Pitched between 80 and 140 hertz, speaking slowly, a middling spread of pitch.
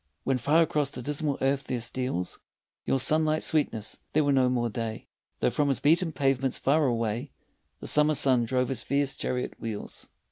No: low, 135 Hz; average, 180 wpm; average, 3.3 semitones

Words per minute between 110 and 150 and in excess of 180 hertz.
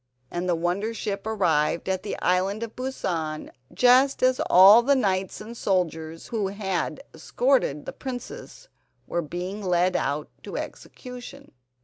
Yes: average, 140 wpm; high, 190 Hz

